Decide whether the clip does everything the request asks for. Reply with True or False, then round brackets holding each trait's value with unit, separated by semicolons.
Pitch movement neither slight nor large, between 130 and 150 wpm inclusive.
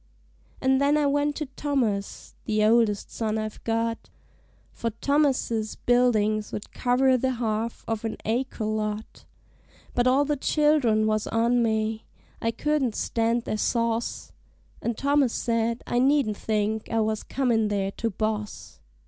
True (3.2 semitones; 140 wpm)